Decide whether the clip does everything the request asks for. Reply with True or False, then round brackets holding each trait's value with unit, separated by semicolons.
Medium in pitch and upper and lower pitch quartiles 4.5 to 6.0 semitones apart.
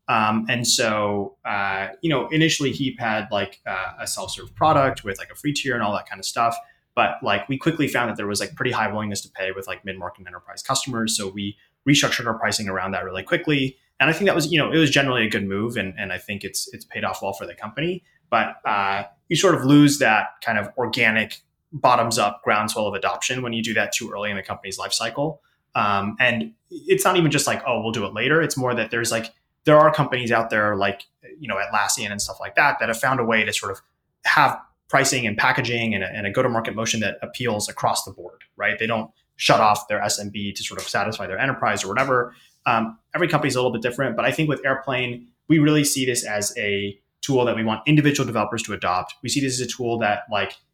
False (115 Hz; 5.0 semitones)